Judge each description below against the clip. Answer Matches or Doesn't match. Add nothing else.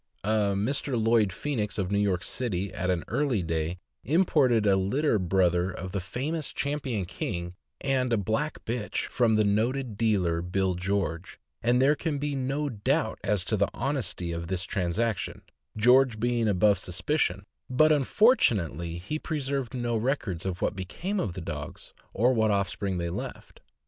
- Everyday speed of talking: Matches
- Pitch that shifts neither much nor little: Doesn't match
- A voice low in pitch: Matches